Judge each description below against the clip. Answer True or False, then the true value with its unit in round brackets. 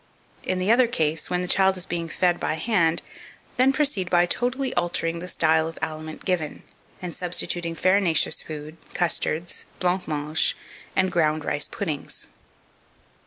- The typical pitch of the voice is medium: True (175 Hz)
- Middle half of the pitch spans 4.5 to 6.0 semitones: False (2.8 semitones)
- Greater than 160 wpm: False (150 wpm)